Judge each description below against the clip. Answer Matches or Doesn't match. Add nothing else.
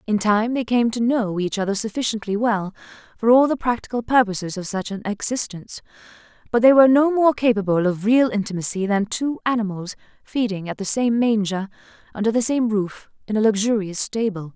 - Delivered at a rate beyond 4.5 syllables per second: Matches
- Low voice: Doesn't match